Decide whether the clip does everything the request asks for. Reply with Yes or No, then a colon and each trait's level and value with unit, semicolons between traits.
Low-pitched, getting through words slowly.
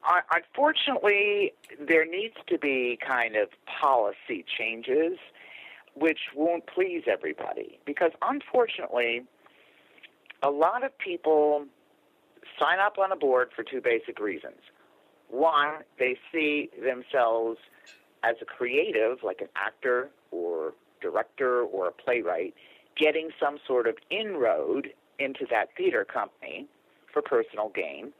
No: medium, 175 Hz; slow, 115 wpm